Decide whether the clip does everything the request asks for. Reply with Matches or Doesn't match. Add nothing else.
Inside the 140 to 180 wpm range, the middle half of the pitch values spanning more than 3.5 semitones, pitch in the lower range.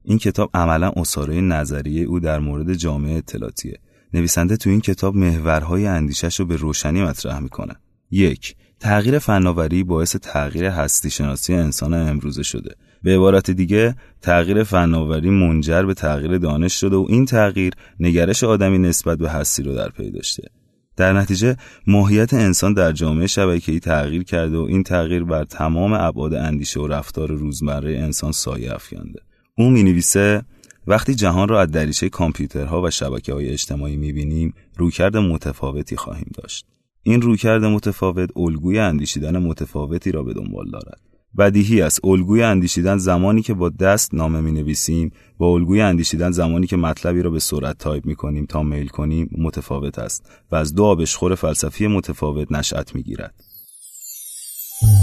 Matches